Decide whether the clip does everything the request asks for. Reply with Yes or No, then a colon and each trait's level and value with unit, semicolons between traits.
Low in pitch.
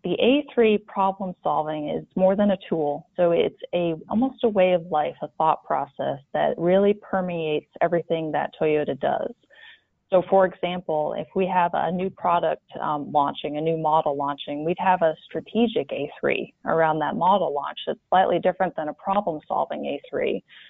No: medium, 175 Hz